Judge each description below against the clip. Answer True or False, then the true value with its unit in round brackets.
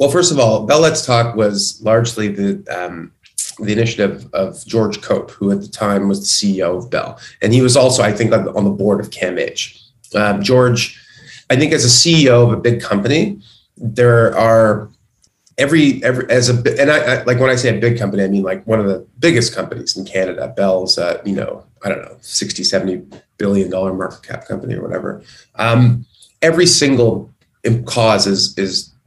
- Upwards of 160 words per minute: True (195 wpm)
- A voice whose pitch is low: True (110 Hz)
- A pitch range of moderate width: True (3.5 semitones)